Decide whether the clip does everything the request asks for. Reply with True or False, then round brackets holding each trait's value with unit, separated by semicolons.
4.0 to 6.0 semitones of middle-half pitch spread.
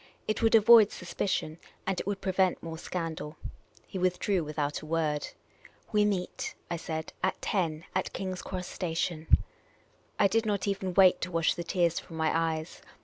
False (3.0 semitones)